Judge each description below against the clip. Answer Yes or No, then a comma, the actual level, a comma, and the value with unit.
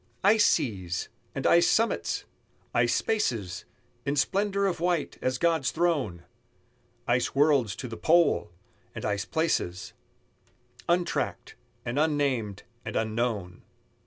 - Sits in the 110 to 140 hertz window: Yes, low, 135 Hz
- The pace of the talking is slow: Yes, slow, 115 wpm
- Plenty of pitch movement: Yes, wide, 8.0 semitones